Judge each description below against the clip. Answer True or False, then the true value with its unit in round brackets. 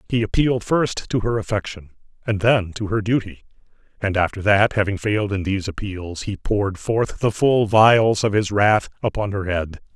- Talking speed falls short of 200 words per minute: True (185 wpm)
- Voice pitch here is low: True (105 Hz)